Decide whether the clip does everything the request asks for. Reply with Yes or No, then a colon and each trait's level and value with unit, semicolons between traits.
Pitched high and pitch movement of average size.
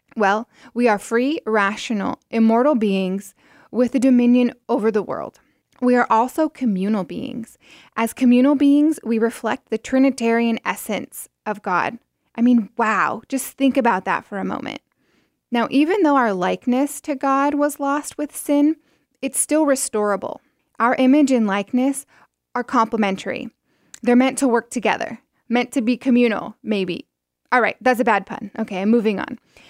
Yes: high, 245 Hz; average, 3.4 semitones